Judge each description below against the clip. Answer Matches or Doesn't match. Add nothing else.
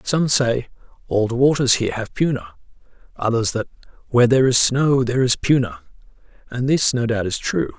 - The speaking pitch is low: Matches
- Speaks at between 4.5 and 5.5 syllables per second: Doesn't match